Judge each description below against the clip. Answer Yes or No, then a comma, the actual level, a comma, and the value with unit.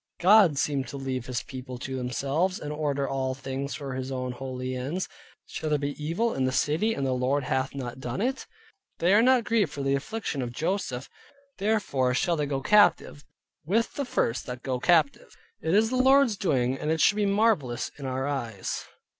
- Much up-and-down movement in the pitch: Yes, wide, 6.5 semitones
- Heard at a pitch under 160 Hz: Yes, medium, 140 Hz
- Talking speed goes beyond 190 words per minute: Yes, average, 200 wpm